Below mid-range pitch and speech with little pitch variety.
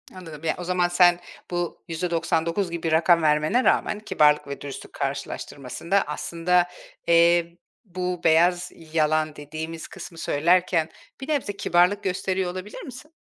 No: medium, 170 Hz; narrow, 2.3 semitones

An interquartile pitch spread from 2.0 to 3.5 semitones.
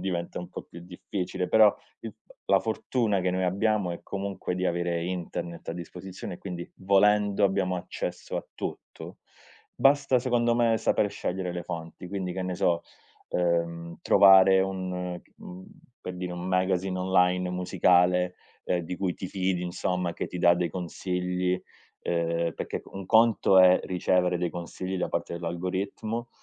No: narrow, 1.5 semitones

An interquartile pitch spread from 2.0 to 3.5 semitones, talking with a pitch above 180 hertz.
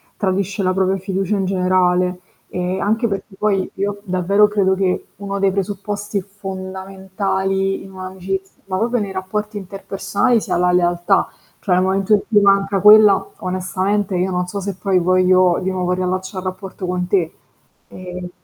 No: narrow, 1.4 semitones; high, 190 Hz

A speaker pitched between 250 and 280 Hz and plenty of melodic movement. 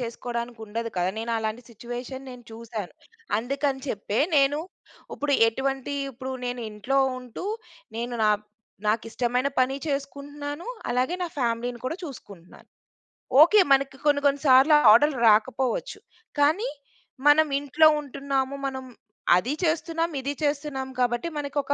No: very high, 265 Hz; average, 3.3 semitones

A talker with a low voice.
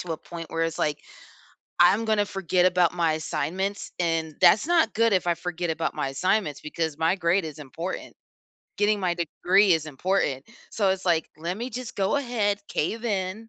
No: medium, 180 Hz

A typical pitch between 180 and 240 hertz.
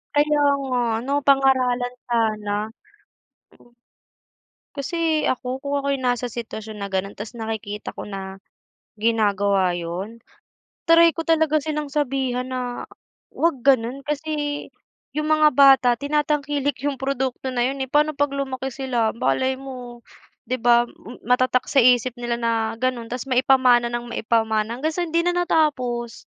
No: very high, 255 Hz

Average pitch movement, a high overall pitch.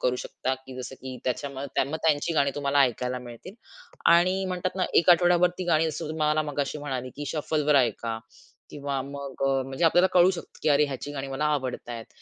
No: average, 3.6 semitones; medium, 145 Hz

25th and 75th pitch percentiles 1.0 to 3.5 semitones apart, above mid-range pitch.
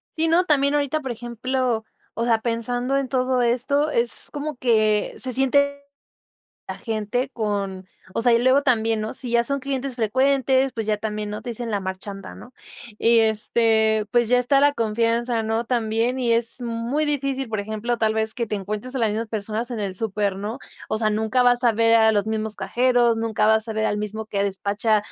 Yes: average, 2.8 semitones; high, 230 Hz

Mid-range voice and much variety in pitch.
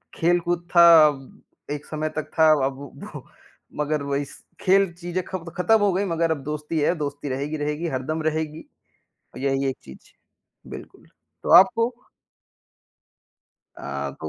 No: medium, 155 Hz; average, 3.4 semitones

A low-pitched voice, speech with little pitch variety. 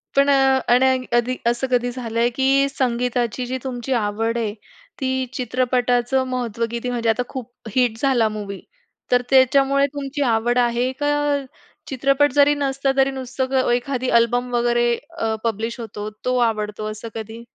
No: high, 245 Hz; narrow, 2.2 semitones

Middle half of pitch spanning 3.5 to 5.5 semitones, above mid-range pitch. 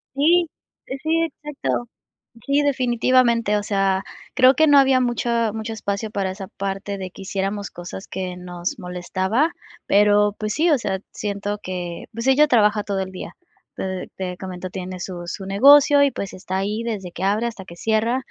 Yes: average, 4.5 semitones; high, 205 Hz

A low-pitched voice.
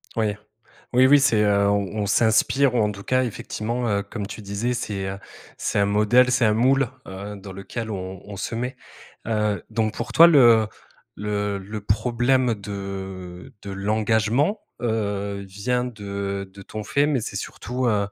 Yes: low, 105 Hz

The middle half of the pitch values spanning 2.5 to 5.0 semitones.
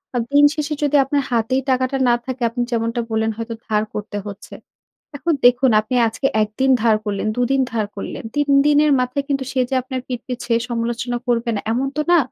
Yes: average, 2.9 semitones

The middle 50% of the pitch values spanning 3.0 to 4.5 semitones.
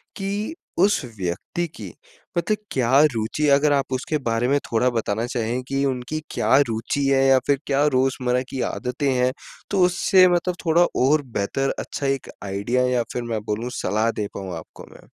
Yes: average, 3.9 semitones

